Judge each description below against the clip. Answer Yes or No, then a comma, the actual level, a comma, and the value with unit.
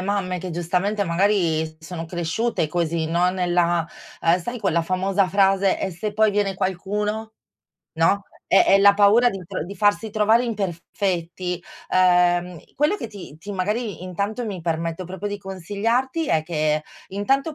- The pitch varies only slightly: No, average, 3.1 semitones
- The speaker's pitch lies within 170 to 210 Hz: Yes, high, 190 Hz